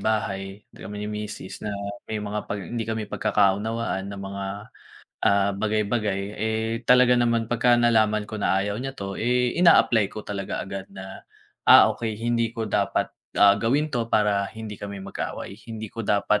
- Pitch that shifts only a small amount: Yes, narrow, 2.3 semitones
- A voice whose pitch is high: No, low, 105 Hz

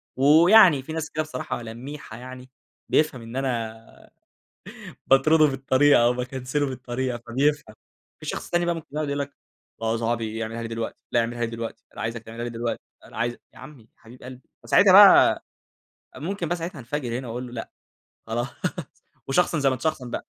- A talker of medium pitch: No, low, 130 Hz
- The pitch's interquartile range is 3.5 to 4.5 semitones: Yes, average, 3.9 semitones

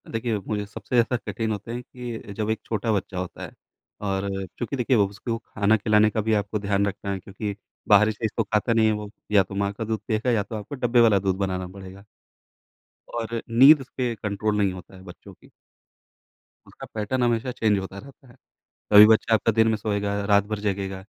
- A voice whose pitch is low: Yes, low, 105 Hz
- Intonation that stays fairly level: Yes, narrow, 2.3 semitones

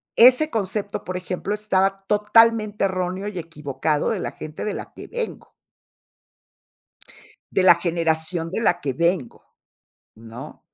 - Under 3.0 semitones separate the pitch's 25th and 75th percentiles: No, average, 4.1 semitones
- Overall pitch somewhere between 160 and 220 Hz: Yes, medium, 185 Hz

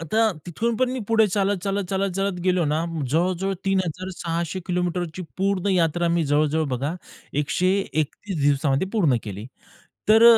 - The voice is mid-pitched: Yes, medium, 180 Hz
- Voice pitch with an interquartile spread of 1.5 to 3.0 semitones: No, average, 3.6 semitones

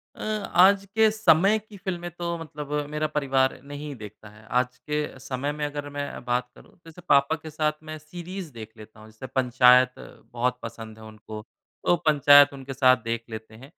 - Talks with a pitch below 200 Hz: Yes, medium, 140 Hz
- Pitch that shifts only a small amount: No, average, 4.1 semitones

